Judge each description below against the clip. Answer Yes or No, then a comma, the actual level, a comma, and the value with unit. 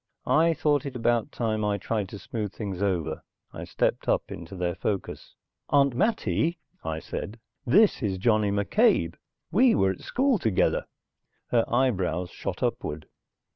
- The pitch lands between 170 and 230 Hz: No, low, 110 Hz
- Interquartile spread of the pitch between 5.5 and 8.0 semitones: Yes, wide, 6.6 semitones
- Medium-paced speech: Yes, average, 150 wpm